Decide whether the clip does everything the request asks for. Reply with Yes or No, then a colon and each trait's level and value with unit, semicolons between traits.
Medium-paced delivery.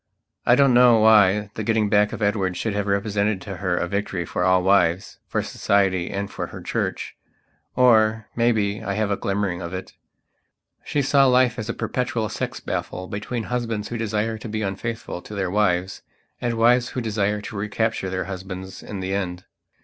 Yes: average, 190 wpm